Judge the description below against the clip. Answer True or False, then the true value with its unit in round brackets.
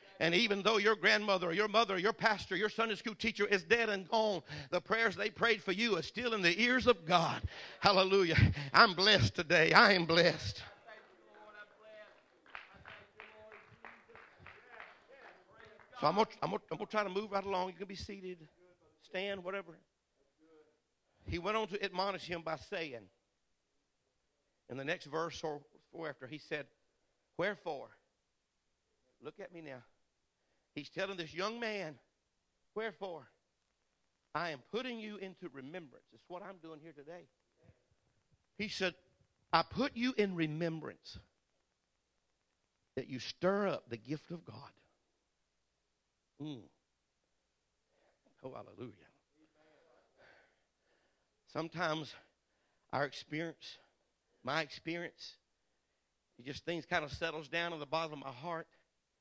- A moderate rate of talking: False (130 wpm)